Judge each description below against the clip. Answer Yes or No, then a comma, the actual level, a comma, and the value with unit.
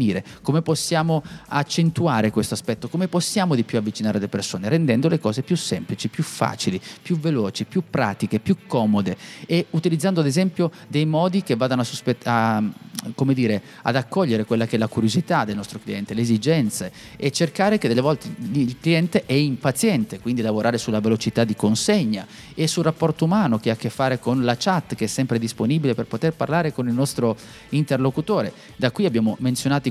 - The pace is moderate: No, fast, 185 wpm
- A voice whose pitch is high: No, low, 135 Hz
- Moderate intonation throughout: No, wide, 6.7 semitones